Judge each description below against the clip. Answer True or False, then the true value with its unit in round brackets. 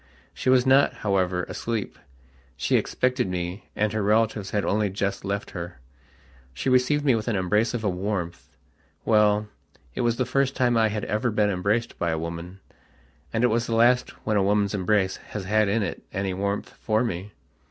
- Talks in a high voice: False (105 Hz)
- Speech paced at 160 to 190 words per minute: True (185 wpm)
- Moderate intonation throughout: True (3.2 semitones)